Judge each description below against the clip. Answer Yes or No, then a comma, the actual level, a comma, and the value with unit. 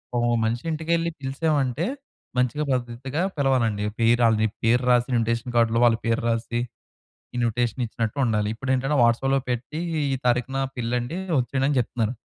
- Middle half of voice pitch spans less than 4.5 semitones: Yes, narrow, 2.6 semitones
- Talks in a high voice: No, low, 125 Hz